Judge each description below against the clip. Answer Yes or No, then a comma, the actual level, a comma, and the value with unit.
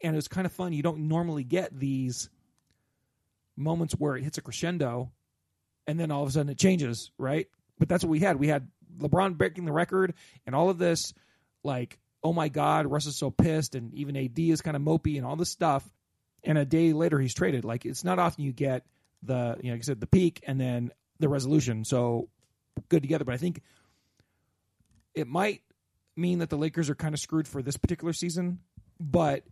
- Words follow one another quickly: Yes, fast, 215 wpm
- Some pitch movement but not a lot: Yes, average, 3.9 semitones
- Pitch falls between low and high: Yes, medium, 150 Hz